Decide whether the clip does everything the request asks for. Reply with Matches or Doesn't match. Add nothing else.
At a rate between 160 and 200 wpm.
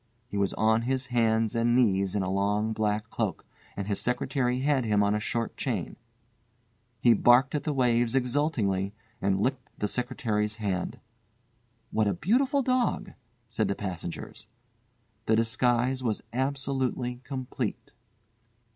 Doesn't match